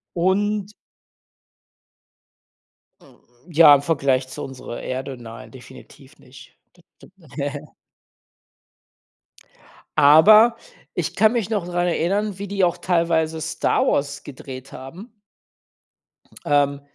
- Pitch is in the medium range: Yes, medium, 155 Hz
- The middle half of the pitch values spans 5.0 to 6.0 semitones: Yes, wide, 5.5 semitones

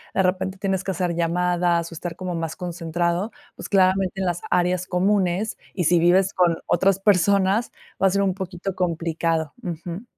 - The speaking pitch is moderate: Yes, medium, 180 Hz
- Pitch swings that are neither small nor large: No, narrow, 1.9 semitones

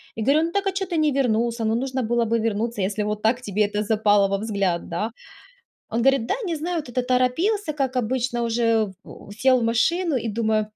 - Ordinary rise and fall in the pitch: Yes, average, 3.8 semitones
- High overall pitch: Yes, high, 235 Hz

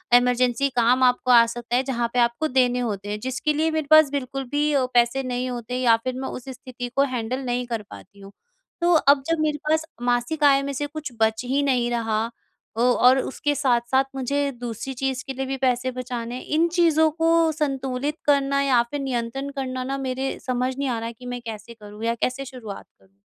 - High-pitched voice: Yes, very high, 255 Hz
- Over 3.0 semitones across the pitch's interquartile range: No, narrow, 2.6 semitones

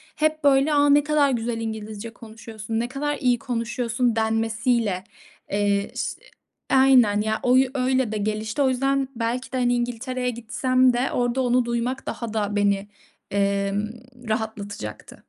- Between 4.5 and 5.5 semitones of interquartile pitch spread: No, average, 3.0 semitones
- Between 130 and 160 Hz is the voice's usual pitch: No, high, 235 Hz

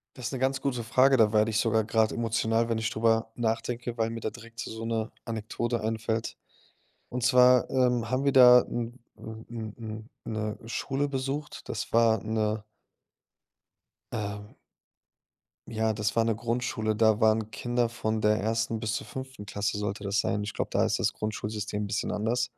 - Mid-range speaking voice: No, low, 115 Hz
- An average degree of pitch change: No, narrow, 1.9 semitones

